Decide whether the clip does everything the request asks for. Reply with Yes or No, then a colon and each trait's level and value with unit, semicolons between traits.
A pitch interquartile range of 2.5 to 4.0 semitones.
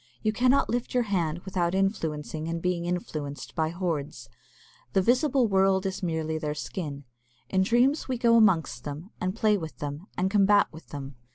No: average, 4.9 semitones